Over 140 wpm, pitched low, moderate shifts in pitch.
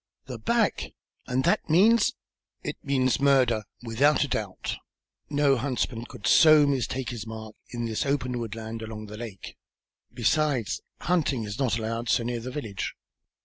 Yes: average, 155 wpm; low, 120 Hz; average, 4.0 semitones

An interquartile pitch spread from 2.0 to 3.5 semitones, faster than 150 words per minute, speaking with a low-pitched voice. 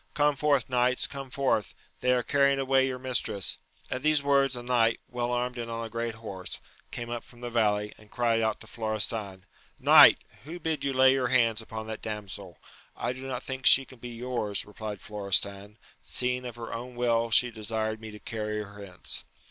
Yes: average, 2.9 semitones; fast, 205 wpm; low, 120 Hz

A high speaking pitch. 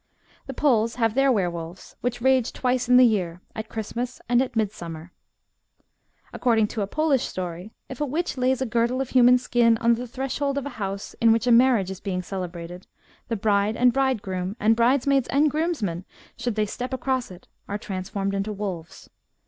Yes: high, 230 Hz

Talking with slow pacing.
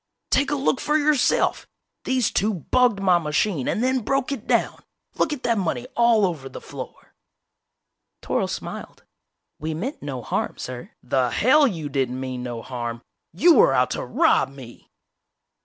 No: average, 170 wpm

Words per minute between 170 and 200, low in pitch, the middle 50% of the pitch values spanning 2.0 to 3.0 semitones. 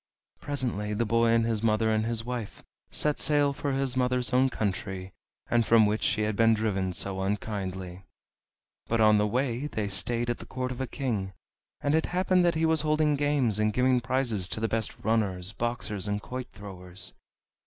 No: average, 185 wpm; low, 115 Hz; average, 3.8 semitones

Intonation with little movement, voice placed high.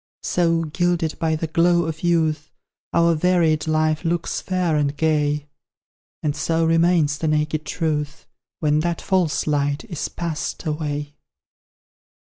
No: narrow, 1.9 semitones; medium, 160 Hz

